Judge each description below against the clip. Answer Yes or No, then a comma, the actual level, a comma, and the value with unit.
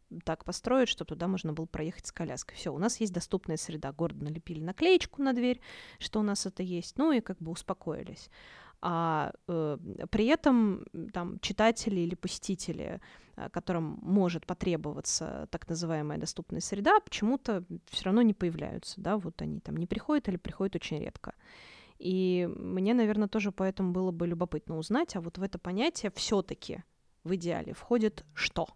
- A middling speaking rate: No, fast, 165 wpm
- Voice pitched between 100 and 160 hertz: No, medium, 185 Hz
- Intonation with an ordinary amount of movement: Yes, average, 4.1 semitones